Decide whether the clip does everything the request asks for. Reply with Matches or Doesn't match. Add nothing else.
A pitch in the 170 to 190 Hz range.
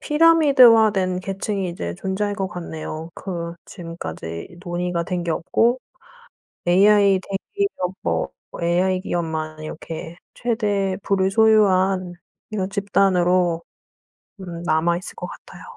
Matches